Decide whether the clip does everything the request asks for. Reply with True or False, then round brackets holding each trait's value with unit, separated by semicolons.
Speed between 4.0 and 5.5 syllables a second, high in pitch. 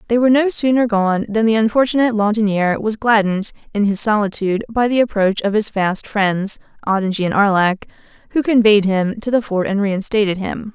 False (5.7 syllables/s; 210 Hz)